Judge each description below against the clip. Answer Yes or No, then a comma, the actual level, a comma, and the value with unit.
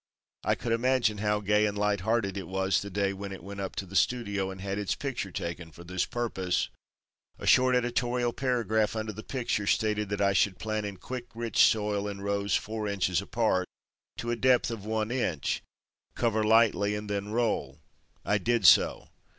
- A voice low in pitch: Yes, low, 105 Hz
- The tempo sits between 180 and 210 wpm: Yes, average, 190 wpm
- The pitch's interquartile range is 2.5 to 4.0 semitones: Yes, average, 2.8 semitones